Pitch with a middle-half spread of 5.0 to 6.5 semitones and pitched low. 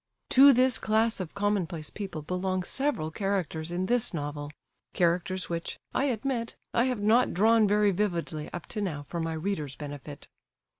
No: average, 5.3 semitones; medium, 185 Hz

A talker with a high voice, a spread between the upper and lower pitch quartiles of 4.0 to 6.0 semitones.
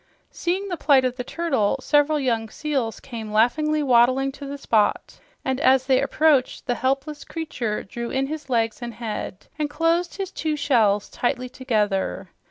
Yes: very high, 265 Hz; average, 4.3 semitones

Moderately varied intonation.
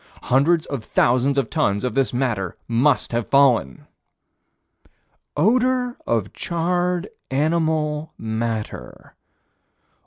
No: wide, 6.0 semitones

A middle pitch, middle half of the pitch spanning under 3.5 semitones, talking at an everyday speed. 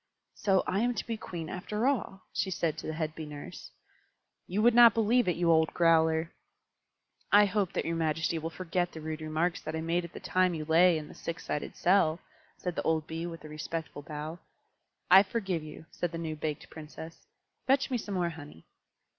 No: medium, 165 Hz; average, 3.1 semitones; fast, 210 wpm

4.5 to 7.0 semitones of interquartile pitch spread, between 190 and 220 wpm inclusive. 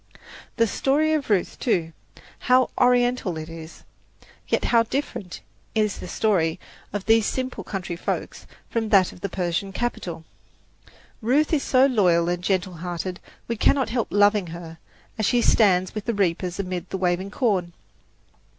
No: average, 4.9 semitones; average, 155 wpm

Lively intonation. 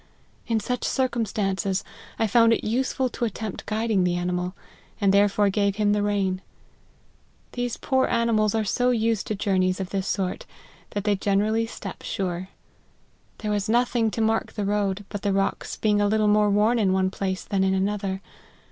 No: narrow, 2.4 semitones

